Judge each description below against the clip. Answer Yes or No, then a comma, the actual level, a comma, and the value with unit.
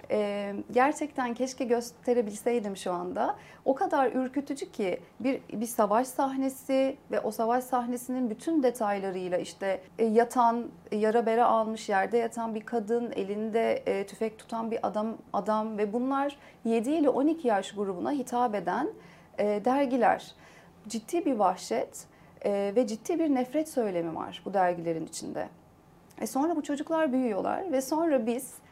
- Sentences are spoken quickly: Yes, fast, 145 wpm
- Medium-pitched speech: No, high, 240 Hz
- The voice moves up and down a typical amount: Yes, average, 4.0 semitones